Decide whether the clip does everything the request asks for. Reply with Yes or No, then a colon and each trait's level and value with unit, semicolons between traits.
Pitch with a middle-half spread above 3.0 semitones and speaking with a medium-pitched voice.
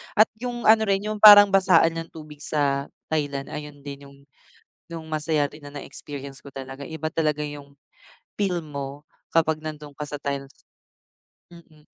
No: narrow, 2.6 semitones; medium, 150 Hz